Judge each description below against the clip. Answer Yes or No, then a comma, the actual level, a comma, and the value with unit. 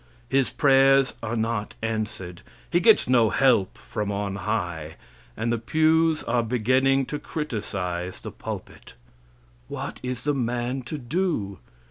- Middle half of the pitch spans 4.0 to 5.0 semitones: Yes, average, 4.6 semitones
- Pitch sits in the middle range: No, low, 120 Hz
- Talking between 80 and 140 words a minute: Yes, slow, 135 wpm